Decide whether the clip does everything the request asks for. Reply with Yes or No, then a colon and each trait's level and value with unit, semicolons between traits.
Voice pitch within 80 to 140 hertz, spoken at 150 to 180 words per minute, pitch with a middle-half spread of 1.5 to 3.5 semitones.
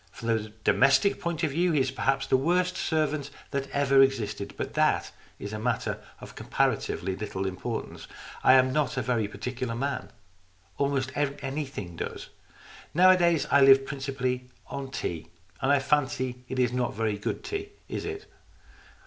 Yes: low, 135 Hz; average, 165 wpm; average, 2.9 semitones